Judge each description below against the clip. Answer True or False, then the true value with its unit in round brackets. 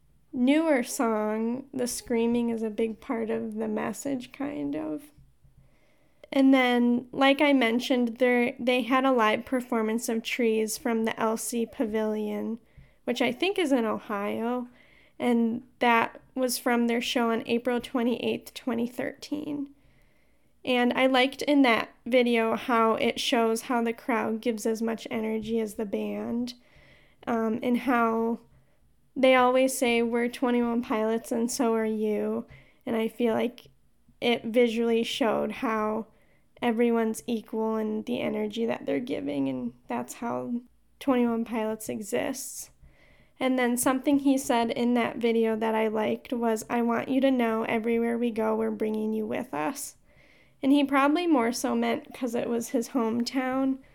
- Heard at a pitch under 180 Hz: False (235 Hz)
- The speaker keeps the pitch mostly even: True (2.3 semitones)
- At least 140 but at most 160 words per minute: True (150 wpm)